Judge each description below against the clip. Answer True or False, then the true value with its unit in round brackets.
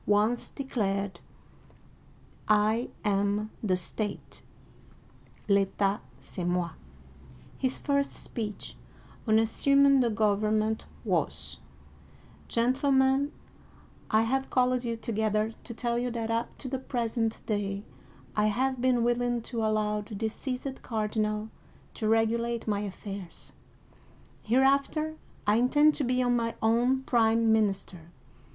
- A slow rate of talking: True (120 wpm)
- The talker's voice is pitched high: True (225 Hz)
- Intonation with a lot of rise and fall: False (2.9 semitones)